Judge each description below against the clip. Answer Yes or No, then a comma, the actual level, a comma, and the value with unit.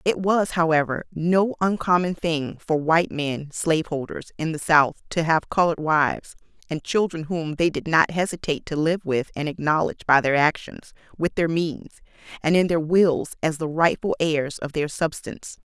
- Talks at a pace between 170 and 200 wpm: Yes, average, 180 wpm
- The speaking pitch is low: No, medium, 160 Hz